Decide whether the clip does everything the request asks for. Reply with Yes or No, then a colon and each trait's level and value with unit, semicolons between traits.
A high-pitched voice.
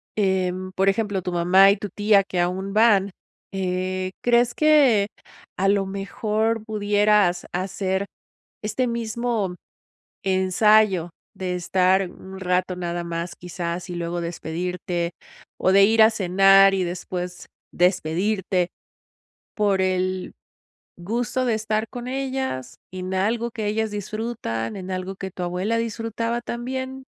Yes: high, 195 Hz